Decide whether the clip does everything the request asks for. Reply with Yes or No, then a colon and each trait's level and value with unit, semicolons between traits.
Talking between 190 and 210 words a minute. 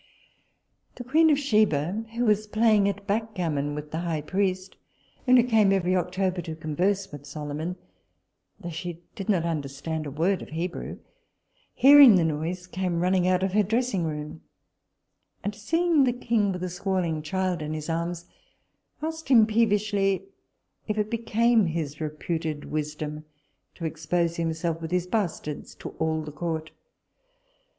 No: average, 155 wpm